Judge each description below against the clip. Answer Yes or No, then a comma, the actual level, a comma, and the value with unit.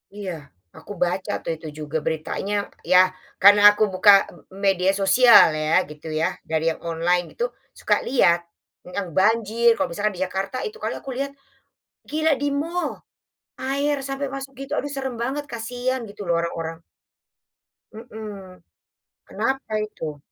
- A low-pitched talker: No, high, 210 Hz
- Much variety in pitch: Yes, wide, 6.7 semitones